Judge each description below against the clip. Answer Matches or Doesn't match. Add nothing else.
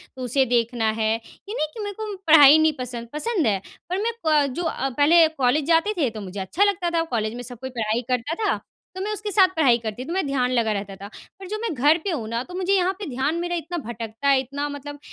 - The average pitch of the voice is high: Matches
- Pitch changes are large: Matches